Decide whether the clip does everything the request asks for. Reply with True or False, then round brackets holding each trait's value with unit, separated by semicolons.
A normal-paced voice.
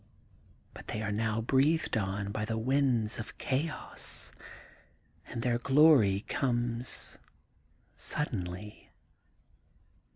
False (95 wpm)